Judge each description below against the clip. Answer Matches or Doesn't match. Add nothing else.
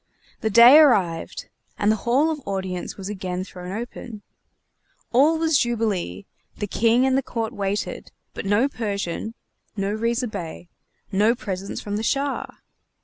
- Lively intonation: Doesn't match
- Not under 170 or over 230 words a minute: Doesn't match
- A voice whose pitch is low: Doesn't match